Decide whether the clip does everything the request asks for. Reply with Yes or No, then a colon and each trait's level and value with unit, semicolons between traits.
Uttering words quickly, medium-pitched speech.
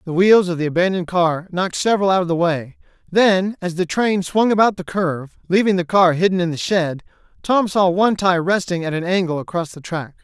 Yes: fast, 225 wpm; medium, 180 Hz